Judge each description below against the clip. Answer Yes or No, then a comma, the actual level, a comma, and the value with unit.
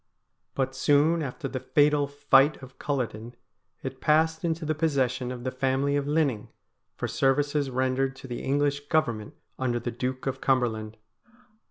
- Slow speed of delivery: No, average, 155 wpm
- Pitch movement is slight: Yes, narrow, 2.2 semitones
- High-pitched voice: No, low, 135 Hz